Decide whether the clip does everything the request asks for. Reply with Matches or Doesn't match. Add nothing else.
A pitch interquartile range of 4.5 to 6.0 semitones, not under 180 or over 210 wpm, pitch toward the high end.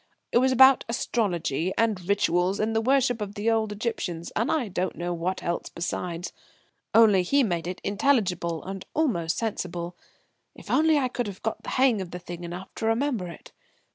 Matches